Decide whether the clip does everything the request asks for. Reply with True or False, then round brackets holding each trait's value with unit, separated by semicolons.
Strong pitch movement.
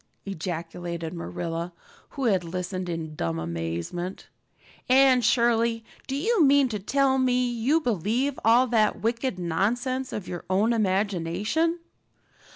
True (6.6 semitones)